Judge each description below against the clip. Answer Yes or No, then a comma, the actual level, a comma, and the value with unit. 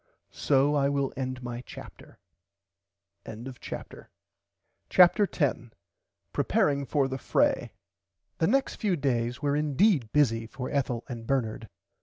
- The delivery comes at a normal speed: No, slow, 125 wpm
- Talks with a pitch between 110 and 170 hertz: Yes, low, 135 Hz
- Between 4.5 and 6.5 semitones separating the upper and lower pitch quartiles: No, average, 3.3 semitones